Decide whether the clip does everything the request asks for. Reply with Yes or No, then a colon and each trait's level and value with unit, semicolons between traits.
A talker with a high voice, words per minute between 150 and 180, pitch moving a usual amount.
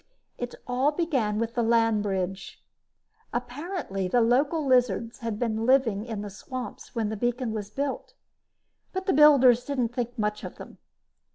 Yes: high, 240 Hz; average, 160 wpm; average, 3.2 semitones